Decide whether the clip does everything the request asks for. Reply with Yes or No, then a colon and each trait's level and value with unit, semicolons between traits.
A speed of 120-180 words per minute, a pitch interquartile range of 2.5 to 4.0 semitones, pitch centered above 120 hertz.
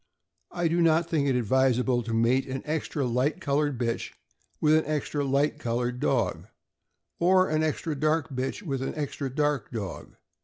Yes: average, 165 wpm; average, 3.6 semitones; medium, 140 Hz